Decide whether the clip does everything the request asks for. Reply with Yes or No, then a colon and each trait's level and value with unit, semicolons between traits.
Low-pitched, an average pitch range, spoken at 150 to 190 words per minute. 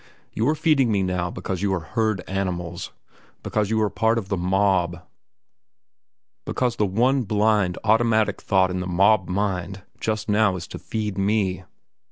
Yes: low, 100 Hz; average, 3.0 semitones; average, 165 wpm